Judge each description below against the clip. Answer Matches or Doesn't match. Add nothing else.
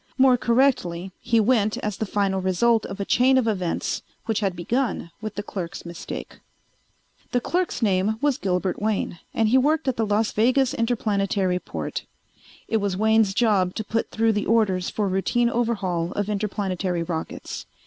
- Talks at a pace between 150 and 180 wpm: Matches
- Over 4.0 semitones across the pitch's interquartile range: Doesn't match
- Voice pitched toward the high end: Matches